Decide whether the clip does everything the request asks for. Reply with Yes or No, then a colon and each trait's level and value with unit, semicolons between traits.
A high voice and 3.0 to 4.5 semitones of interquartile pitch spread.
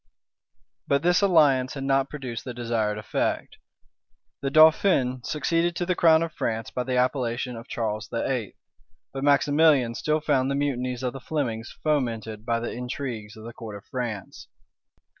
No: low, 130 Hz; average, 3.9 semitones